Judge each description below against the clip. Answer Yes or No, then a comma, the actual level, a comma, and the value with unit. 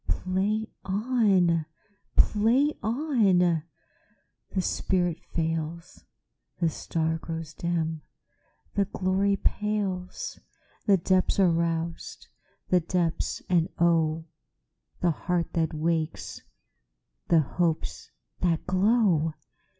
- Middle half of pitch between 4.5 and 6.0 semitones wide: No, average, 3.2 semitones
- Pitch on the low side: No, medium, 175 Hz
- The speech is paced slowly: Yes, slow, 80 wpm